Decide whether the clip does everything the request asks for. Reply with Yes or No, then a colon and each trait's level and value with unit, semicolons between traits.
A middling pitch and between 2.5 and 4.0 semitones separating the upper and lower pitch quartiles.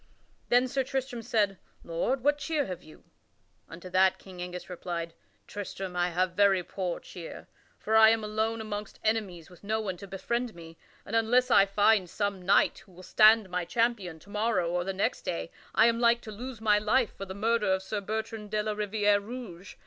No: high, 205 Hz; average, 3.4 semitones